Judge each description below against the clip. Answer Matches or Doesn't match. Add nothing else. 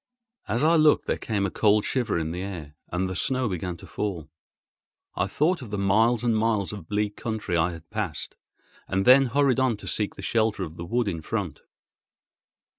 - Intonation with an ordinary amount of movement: Matches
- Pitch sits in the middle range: Doesn't match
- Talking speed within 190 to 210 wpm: Matches